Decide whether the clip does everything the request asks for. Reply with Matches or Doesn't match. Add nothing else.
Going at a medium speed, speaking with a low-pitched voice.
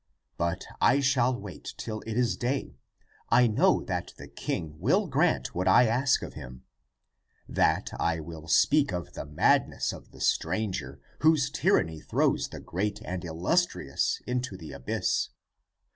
Matches